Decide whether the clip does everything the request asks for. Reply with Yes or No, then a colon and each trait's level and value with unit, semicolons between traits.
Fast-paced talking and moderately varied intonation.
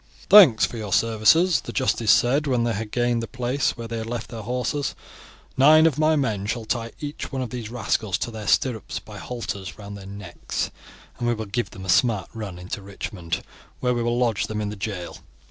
Yes: fast, 215 wpm; average, 3.2 semitones